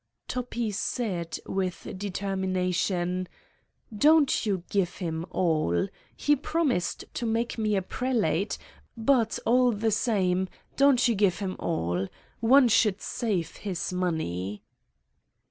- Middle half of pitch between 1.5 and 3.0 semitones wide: No, average, 4.6 semitones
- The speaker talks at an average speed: No, slow, 115 wpm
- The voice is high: Yes, high, 195 Hz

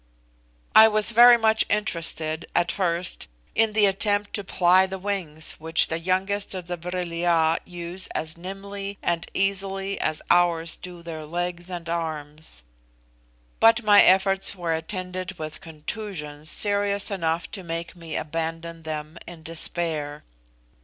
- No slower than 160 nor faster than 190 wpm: No, average, 140 wpm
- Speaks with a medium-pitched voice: Yes, medium, 175 Hz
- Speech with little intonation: No, average, 3.2 semitones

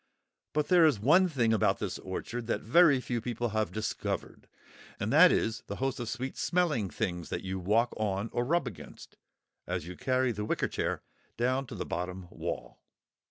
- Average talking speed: Yes, average, 185 wpm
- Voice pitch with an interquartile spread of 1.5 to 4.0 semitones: No, average, 4.6 semitones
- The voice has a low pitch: Yes, low, 115 Hz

